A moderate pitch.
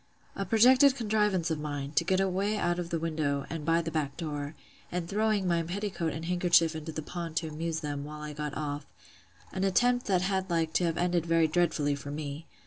Yes: medium, 165 Hz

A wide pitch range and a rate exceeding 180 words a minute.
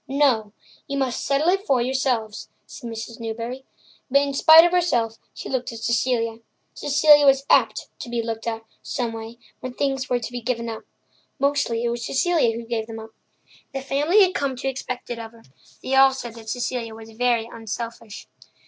No: average, 3.1 semitones; average, 190 wpm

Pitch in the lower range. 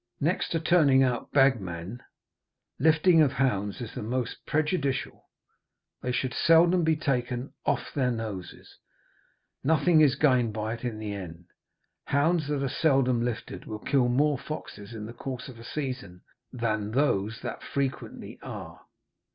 Yes: low, 130 Hz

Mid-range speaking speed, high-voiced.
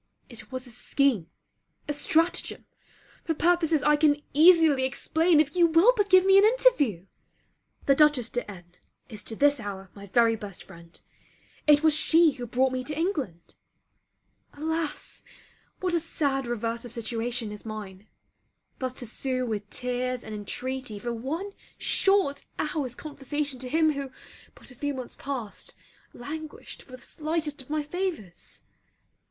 Yes: average, 155 wpm; very high, 270 Hz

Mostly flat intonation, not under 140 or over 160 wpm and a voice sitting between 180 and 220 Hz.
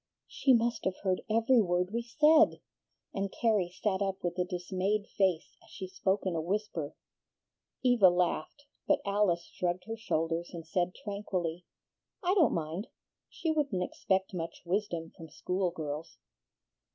No: average, 3.5 semitones; average, 150 wpm; high, 190 Hz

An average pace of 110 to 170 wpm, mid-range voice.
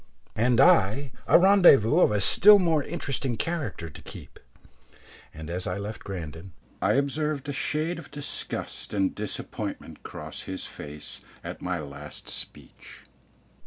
No: average, 140 wpm; low, 115 Hz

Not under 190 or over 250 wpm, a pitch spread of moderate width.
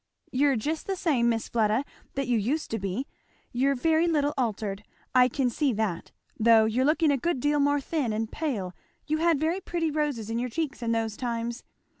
Yes: average, 200 wpm; average, 4.9 semitones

